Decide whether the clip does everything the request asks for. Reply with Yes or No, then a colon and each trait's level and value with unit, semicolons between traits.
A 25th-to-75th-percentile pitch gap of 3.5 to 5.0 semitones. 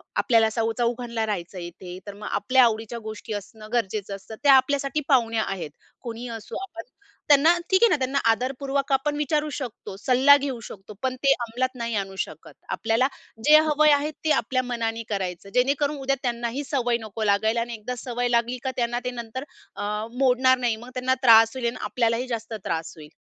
No: average, 3.1 semitones